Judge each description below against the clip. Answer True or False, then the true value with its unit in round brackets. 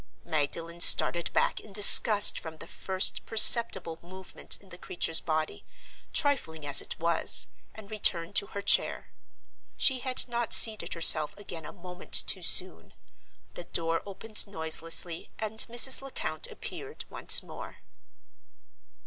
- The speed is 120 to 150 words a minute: True (135 wpm)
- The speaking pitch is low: False (185 Hz)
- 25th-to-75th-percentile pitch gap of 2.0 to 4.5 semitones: False (4.9 semitones)